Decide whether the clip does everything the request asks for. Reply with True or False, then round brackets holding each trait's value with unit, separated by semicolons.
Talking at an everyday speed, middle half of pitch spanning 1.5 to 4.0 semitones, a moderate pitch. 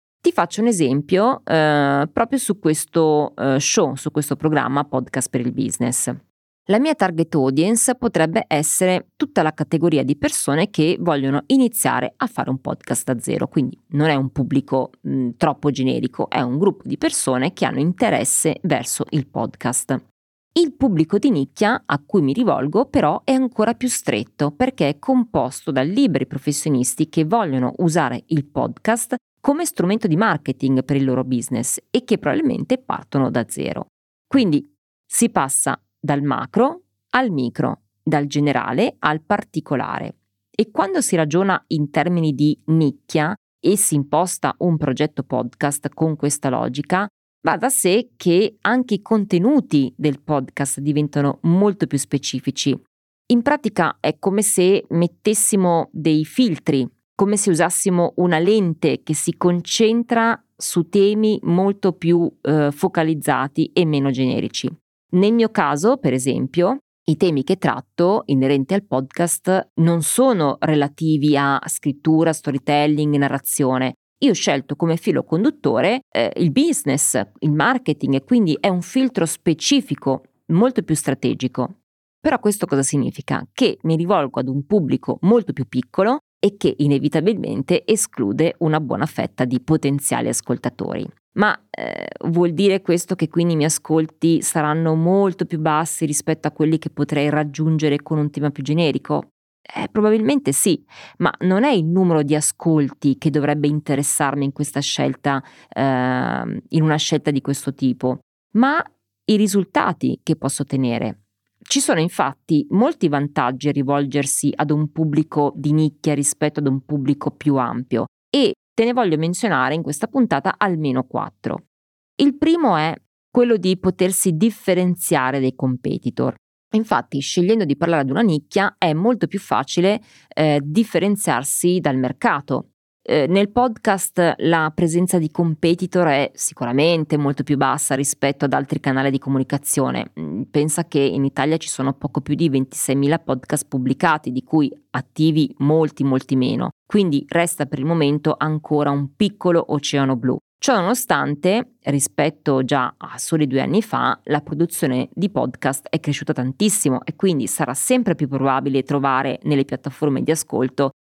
False (150 wpm; 5.3 semitones; 155 Hz)